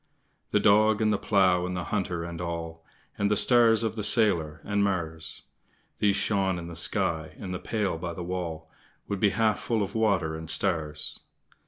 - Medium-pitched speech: No, very low, 90 Hz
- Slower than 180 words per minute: No, average, 190 wpm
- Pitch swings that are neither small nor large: Yes, average, 3.9 semitones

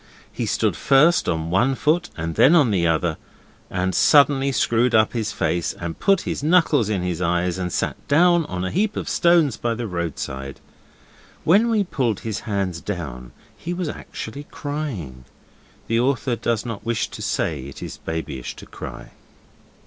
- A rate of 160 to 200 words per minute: Yes, average, 170 wpm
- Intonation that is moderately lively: No, wide, 8.9 semitones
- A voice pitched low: Yes, low, 110 Hz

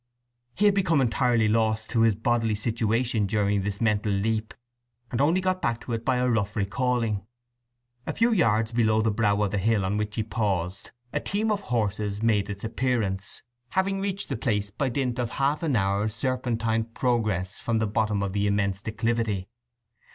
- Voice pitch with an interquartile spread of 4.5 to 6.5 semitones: No, average, 3.2 semitones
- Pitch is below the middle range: Yes, low, 110 Hz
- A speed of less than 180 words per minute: No, average, 185 wpm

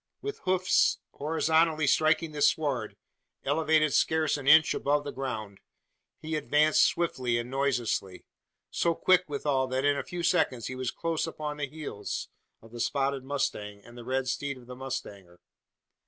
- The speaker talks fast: No, average, 160 wpm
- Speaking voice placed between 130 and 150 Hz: Yes, medium, 140 Hz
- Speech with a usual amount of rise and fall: Yes, average, 3.7 semitones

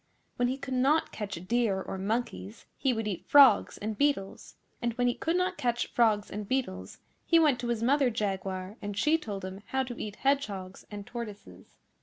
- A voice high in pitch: Yes, high, 230 Hz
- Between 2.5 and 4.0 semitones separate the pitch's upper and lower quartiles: No, average, 4.7 semitones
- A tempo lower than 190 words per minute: No, average, 195 wpm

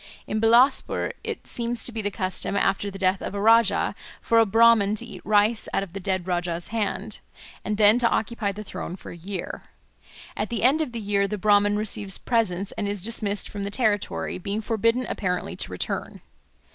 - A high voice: Yes, high, 205 Hz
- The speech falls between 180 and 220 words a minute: Yes, average, 200 wpm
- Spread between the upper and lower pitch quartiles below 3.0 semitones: Yes, narrow, 2.6 semitones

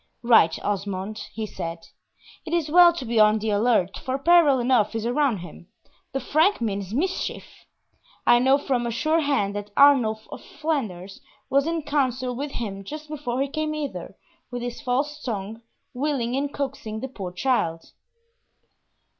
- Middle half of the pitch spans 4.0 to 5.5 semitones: Yes, average, 5.2 semitones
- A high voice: Yes, high, 245 Hz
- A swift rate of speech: No, average, 165 wpm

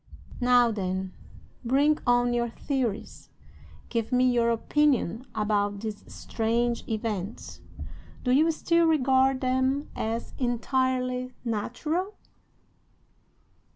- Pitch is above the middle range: Yes, high, 245 Hz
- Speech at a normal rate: No, slow, 95 wpm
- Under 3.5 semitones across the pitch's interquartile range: Yes, average, 2.7 semitones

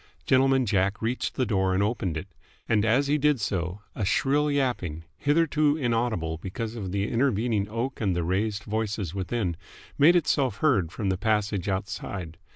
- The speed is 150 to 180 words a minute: Yes, average, 165 wpm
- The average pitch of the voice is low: Yes, low, 110 Hz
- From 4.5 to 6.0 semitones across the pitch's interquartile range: Yes, average, 5.3 semitones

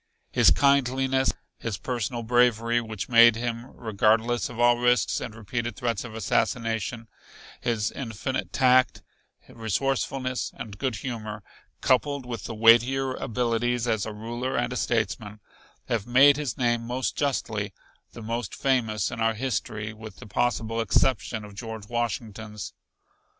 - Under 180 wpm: Yes, average, 140 wpm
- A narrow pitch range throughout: Yes, narrow, 2.1 semitones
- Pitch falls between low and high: No, low, 115 Hz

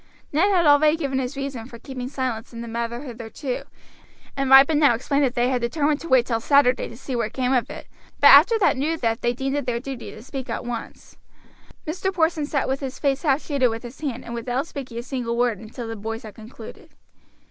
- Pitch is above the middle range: Yes, very high, 260 Hz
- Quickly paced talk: Yes, fast, 235 wpm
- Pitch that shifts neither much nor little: Yes, average, 3.2 semitones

